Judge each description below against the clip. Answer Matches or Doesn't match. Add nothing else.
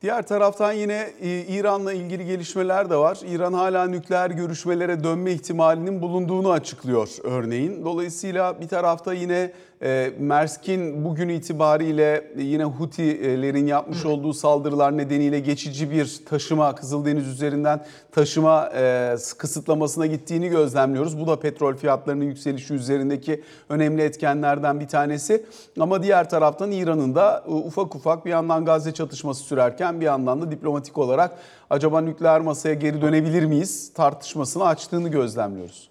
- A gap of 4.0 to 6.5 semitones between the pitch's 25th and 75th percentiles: Doesn't match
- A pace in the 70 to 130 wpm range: Matches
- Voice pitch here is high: Doesn't match